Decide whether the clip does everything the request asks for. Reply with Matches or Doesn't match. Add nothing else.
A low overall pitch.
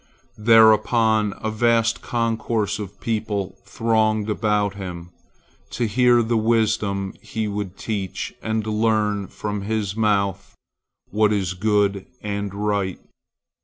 Matches